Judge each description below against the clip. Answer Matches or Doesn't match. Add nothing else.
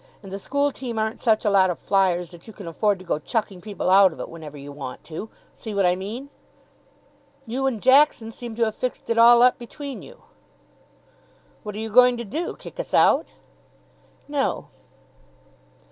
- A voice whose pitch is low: Doesn't match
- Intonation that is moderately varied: Matches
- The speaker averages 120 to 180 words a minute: Doesn't match